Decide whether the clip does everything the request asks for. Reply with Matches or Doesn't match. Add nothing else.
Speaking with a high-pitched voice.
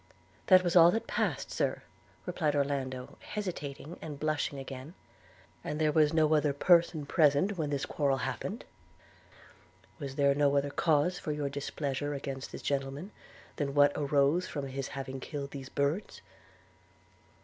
Doesn't match